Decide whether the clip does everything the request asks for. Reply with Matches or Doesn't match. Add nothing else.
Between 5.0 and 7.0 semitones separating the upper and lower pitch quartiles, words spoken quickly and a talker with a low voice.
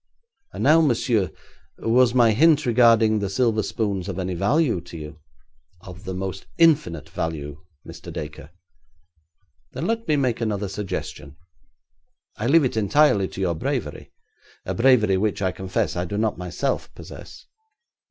Doesn't match